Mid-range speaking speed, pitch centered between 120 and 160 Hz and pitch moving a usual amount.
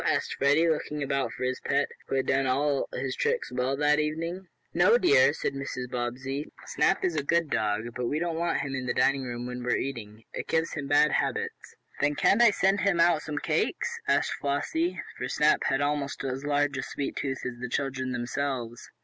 No: fast, 210 wpm; medium, 140 Hz; average, 3.1 semitones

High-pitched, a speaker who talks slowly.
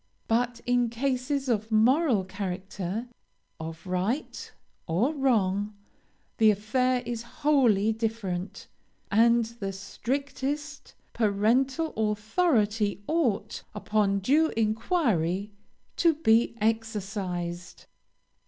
Yes: high, 225 Hz; slow, 90 wpm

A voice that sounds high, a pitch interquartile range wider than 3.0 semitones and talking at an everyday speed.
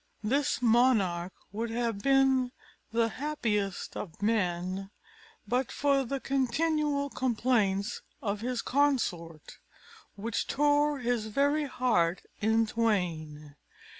No: high, 230 Hz; average, 5.3 semitones; slow, 105 wpm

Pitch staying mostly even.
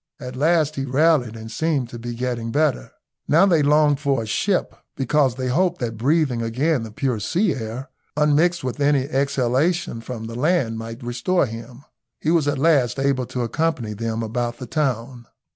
No: average, 4.4 semitones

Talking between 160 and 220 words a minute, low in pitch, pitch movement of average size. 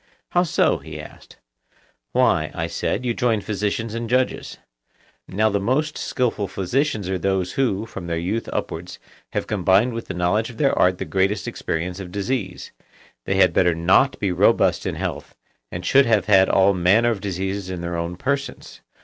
Yes: average, 180 wpm; low, 100 Hz; average, 4.1 semitones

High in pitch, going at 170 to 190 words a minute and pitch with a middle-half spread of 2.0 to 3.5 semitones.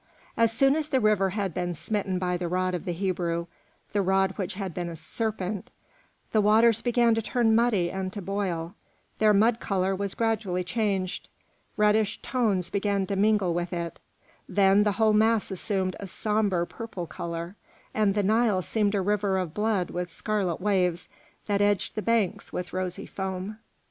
Yes: high, 195 Hz; average, 175 wpm; average, 2.8 semitones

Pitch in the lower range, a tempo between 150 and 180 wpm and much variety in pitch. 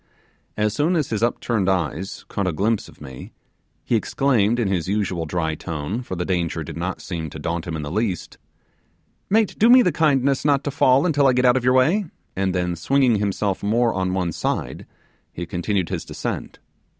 No: low, 100 Hz; average, 200 wpm; wide, 6.6 semitones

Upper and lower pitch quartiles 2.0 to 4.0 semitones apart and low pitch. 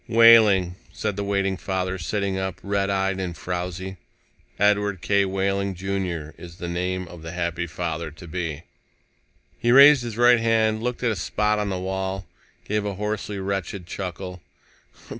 Yes: narrow, 2.4 semitones; very low, 95 Hz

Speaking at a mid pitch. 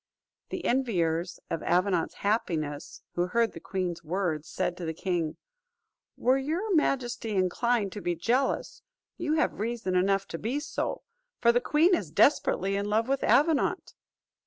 No: high, 205 Hz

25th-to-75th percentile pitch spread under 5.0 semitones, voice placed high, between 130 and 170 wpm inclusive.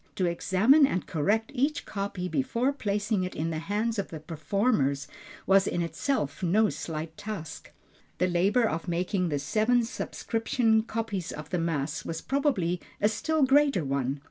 No: wide, 5.5 semitones; high, 195 Hz; average, 160 wpm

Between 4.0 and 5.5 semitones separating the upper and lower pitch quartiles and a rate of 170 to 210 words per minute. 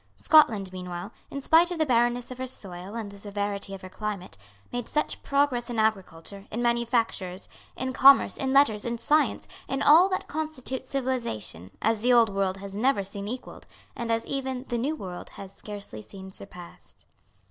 Yes: average, 4.8 semitones; average, 180 wpm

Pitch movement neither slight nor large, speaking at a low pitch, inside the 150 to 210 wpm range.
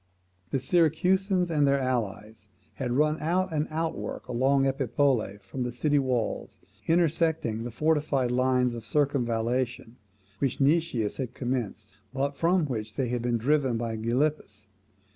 No: average, 4.3 semitones; low, 130 Hz; average, 140 wpm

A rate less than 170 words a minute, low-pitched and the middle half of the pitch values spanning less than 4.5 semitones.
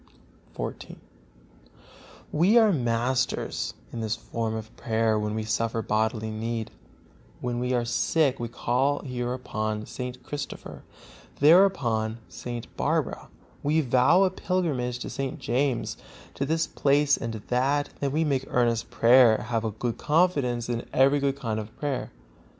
Yes: average, 150 wpm; low, 125 Hz; average, 3.8 semitones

